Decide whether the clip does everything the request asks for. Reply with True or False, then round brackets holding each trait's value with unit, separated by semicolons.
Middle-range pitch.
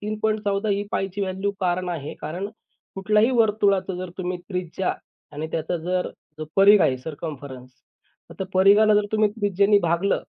False (195 Hz)